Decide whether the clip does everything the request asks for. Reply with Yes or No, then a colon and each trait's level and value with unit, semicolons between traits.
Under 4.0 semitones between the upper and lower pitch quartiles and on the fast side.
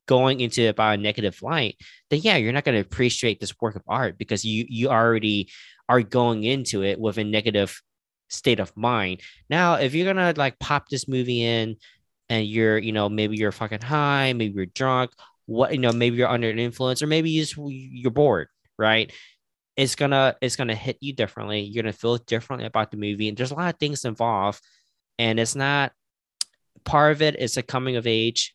Yes: average, 3.5 semitones; fast, 210 wpm